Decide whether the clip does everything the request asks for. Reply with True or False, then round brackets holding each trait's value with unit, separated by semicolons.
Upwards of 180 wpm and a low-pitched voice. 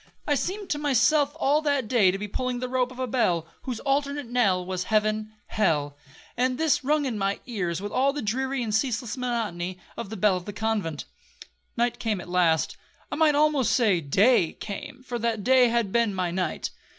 False (200 wpm; 235 Hz)